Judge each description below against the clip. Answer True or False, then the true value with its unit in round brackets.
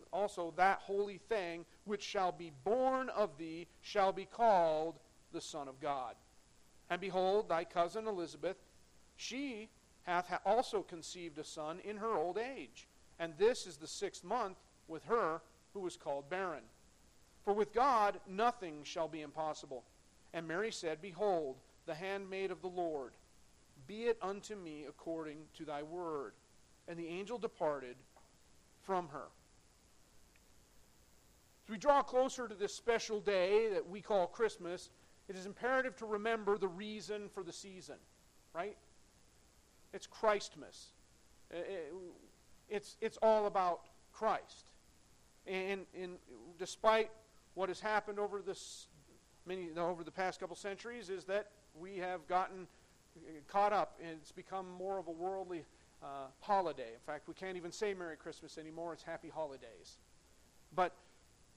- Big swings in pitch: False (3.9 semitones)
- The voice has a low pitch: False (185 Hz)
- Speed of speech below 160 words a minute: True (145 wpm)